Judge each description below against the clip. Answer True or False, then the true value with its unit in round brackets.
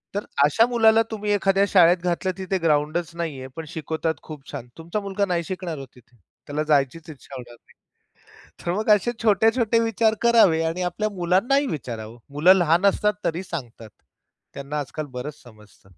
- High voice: False (170 Hz)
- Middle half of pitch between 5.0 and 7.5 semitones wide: True (5.4 semitones)